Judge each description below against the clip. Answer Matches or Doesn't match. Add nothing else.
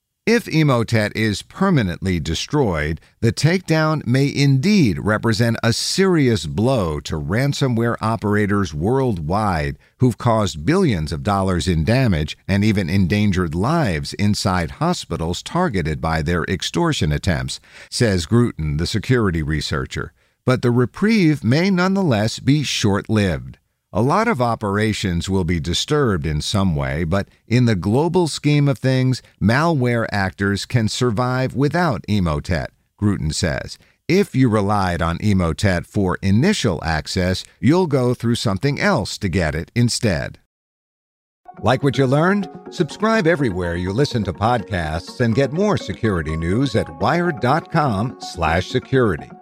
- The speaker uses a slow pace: Matches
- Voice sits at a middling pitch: Doesn't match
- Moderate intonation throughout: Doesn't match